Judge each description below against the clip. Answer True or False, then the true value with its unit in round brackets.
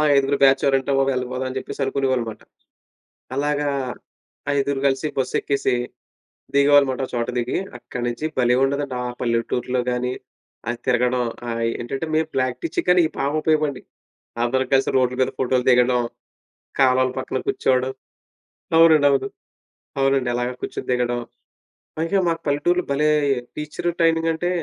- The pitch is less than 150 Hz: True (135 Hz)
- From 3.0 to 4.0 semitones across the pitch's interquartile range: False (2.5 semitones)